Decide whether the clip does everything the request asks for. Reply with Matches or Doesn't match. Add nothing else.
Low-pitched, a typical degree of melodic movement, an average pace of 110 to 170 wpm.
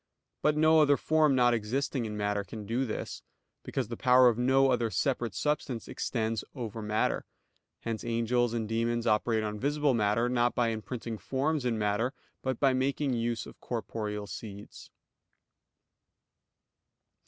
Matches